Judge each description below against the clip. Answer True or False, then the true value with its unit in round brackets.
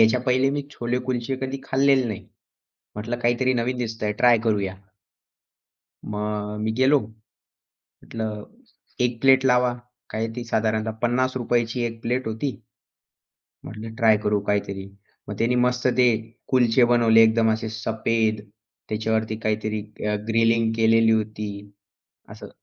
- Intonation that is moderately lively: False (2.2 semitones)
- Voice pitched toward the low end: True (115 Hz)